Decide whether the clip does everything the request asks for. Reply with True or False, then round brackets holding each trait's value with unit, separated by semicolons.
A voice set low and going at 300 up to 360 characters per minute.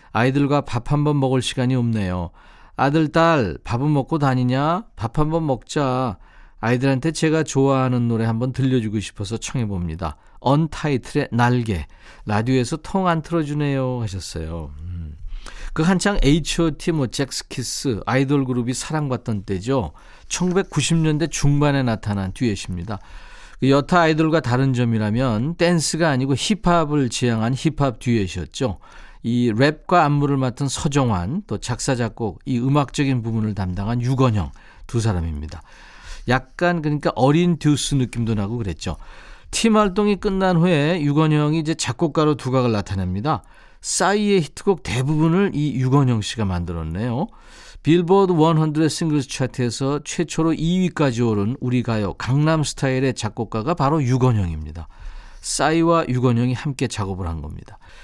True (130 Hz; 315 characters per minute)